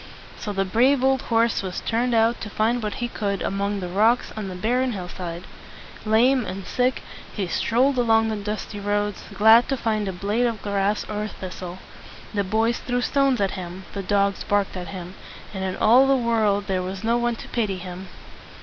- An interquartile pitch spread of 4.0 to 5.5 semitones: No, average, 3.4 semitones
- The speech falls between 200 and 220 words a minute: Yes, fast, 205 wpm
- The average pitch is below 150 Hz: No, high, 210 Hz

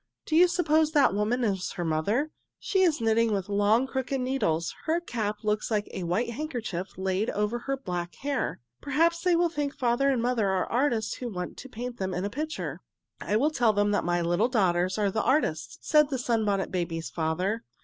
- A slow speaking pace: No, average, 200 wpm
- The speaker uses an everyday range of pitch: No, wide, 6.0 semitones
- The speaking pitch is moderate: No, high, 225 Hz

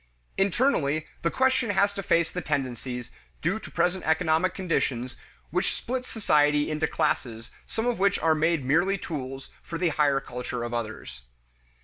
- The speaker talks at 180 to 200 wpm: No, average, 155 wpm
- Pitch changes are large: Yes, wide, 5.9 semitones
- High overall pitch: No, medium, 160 Hz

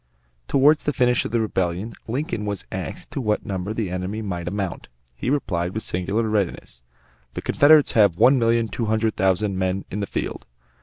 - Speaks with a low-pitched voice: Yes, low, 105 Hz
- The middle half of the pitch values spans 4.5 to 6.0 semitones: No, average, 3.7 semitones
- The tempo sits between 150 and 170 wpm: No, average, 185 wpm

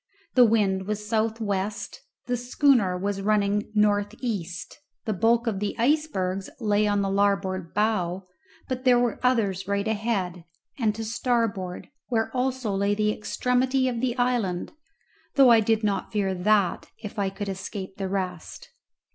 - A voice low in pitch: No, high, 210 Hz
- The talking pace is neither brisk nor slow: Yes, average, 155 wpm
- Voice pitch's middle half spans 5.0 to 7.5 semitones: No, average, 3.2 semitones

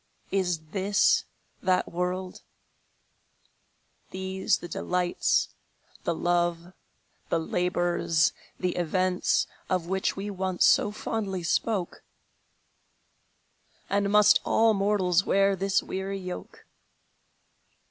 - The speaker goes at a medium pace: No, slow, 95 wpm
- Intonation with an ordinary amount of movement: No, narrow, 1.8 semitones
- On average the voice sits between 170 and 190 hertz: Yes, medium, 185 Hz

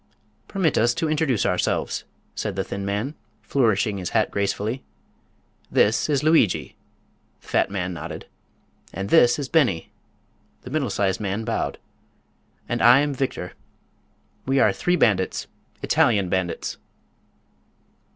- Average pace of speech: No, slow, 125 wpm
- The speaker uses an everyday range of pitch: No, wide, 5.8 semitones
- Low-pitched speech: Yes, low, 110 Hz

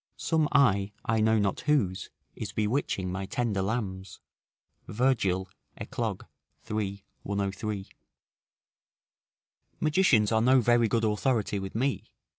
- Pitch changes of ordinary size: Yes, average, 3.9 semitones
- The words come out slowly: Yes, slow, 110 wpm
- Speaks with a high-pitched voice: No, low, 110 Hz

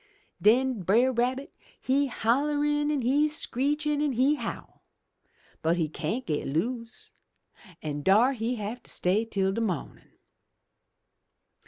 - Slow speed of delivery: Yes, slow, 130 wpm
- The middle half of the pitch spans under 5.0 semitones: No, wide, 5.5 semitones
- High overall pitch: Yes, high, 245 Hz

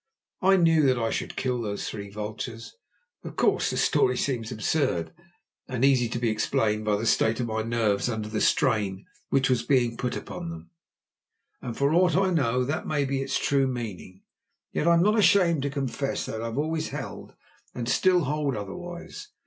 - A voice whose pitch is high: No, low, 125 Hz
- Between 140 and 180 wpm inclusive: No, average, 190 wpm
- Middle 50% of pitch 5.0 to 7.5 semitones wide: Yes, average, 5.3 semitones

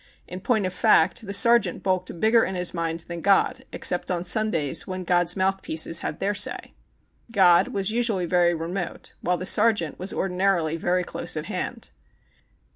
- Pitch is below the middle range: No, medium, 185 Hz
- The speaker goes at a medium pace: Yes, average, 170 wpm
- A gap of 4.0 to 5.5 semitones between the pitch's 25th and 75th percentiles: No, narrow, 2.5 semitones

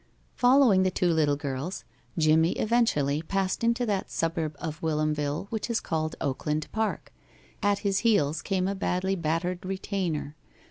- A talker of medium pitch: Yes, medium, 175 Hz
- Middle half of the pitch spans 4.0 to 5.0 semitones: Yes, average, 4.4 semitones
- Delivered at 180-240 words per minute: No, average, 145 wpm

